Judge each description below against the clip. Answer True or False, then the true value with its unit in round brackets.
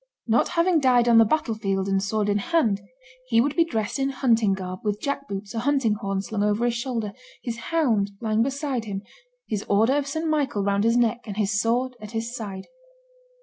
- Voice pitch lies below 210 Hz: False (225 Hz)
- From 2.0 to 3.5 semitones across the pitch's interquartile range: False (4.2 semitones)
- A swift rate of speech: True (210 wpm)